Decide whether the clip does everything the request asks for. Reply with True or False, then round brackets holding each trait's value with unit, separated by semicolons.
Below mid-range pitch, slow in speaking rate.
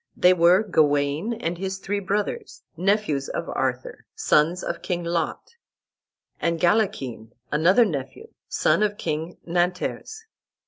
False (180 Hz; 125 wpm)